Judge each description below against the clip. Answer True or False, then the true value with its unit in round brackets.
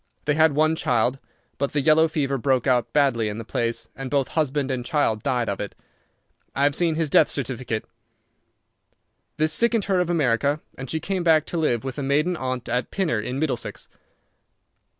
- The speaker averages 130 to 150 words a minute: False (190 wpm)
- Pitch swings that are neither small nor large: True (4.1 semitones)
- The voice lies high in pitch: False (140 Hz)